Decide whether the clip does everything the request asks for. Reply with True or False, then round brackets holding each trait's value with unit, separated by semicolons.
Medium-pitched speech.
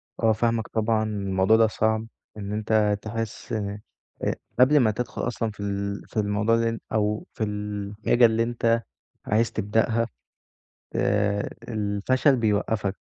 False (110 Hz)